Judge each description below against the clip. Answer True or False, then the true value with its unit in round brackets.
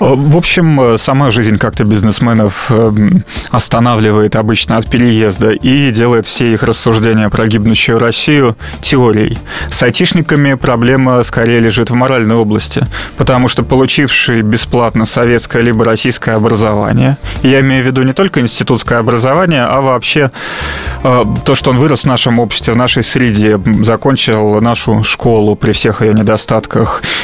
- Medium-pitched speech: False (120 Hz)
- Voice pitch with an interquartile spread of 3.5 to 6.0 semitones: False (2.9 semitones)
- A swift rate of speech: False (135 wpm)